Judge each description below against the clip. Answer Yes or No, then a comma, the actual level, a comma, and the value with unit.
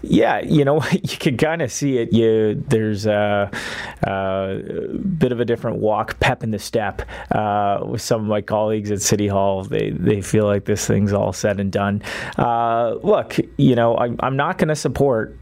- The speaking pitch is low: Yes, low, 110 Hz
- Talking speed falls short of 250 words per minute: Yes, average, 200 wpm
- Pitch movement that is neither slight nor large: Yes, average, 3.7 semitones